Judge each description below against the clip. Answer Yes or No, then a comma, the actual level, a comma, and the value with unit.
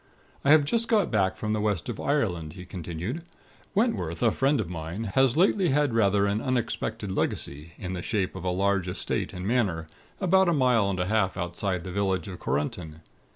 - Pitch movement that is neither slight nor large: No, wide, 6.2 semitones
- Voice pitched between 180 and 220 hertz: No, low, 100 Hz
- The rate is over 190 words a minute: Yes, average, 200 wpm